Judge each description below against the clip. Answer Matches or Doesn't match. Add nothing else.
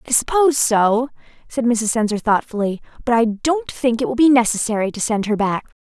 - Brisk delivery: Doesn't match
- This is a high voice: Matches